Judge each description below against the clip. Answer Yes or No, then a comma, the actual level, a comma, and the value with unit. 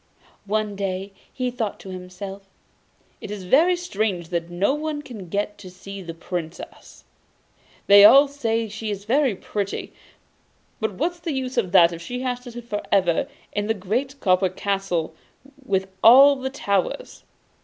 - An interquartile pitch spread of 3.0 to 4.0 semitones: No, average, 5.1 semitones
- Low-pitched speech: No, high, 205 Hz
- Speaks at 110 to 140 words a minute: No, average, 165 wpm